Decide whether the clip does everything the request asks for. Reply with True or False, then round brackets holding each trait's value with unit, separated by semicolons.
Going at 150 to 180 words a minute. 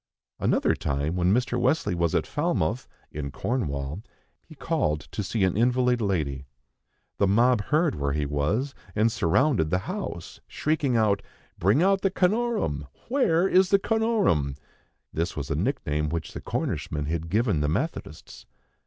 True (155 wpm)